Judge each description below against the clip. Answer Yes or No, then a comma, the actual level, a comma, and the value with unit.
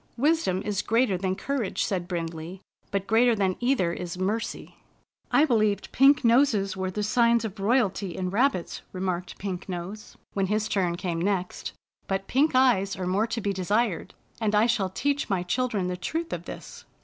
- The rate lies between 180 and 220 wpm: Yes, average, 190 wpm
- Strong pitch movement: No, average, 4.1 semitones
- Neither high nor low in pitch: No, high, 200 Hz